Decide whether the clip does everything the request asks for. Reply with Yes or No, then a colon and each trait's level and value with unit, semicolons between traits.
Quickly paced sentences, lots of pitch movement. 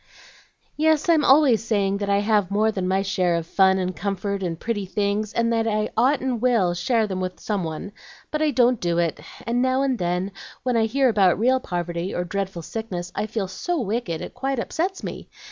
No: fast, 215 wpm; average, 4.7 semitones